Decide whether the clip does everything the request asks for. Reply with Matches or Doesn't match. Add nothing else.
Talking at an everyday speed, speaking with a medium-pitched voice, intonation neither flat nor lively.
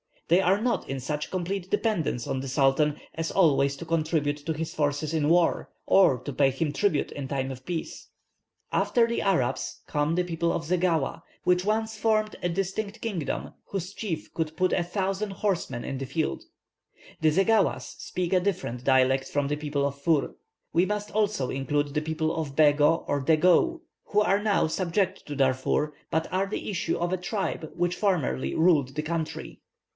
Matches